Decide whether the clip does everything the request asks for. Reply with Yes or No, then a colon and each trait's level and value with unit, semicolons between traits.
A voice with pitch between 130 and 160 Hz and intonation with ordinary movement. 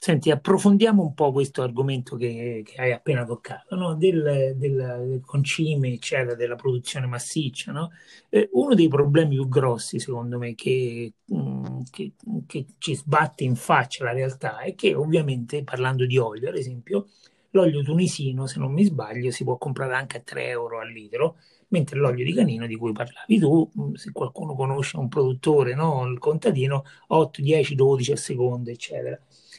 Yes: low, 135 Hz; average, 4.0 semitones